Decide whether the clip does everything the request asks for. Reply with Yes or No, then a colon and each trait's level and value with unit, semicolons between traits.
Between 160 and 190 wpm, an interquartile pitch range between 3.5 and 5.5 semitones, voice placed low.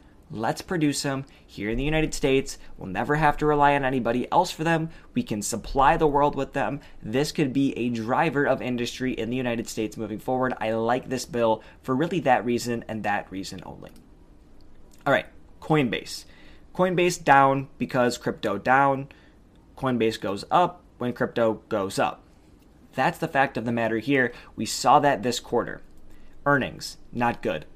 Yes: average, 175 wpm; average, 3.9 semitones; low, 125 Hz